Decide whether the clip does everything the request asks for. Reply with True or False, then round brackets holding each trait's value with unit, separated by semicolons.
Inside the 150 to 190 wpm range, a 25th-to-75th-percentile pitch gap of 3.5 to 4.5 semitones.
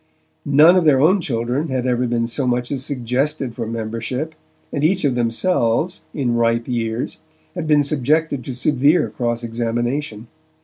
True (160 wpm; 4.1 semitones)